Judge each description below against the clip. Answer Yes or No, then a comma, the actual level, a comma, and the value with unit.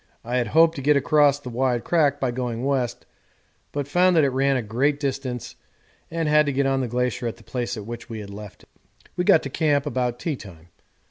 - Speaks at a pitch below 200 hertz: Yes, low, 135 Hz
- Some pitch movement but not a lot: Yes, average, 3.1 semitones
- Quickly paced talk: Yes, fast, 230 wpm